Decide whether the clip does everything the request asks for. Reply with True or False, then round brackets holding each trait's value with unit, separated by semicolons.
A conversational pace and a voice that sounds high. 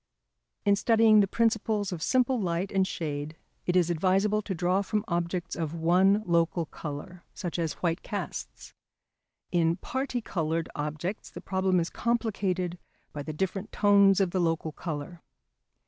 False (150 wpm; 180 Hz)